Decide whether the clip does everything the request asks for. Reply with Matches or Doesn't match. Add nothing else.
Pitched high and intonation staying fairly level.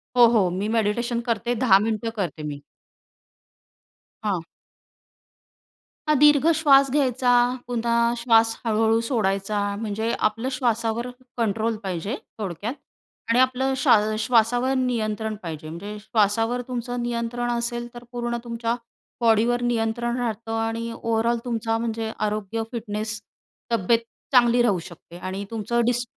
Matches